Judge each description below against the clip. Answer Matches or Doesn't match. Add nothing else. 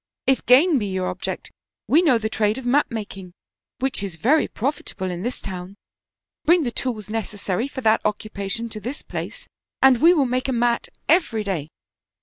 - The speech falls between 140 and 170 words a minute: Doesn't match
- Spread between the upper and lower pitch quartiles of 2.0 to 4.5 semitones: Doesn't match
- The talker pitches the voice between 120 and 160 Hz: Doesn't match